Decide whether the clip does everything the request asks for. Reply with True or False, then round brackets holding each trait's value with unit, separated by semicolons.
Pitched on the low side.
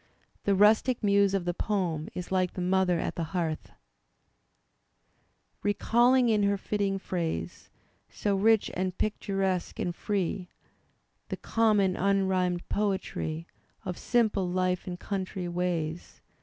False (190 Hz)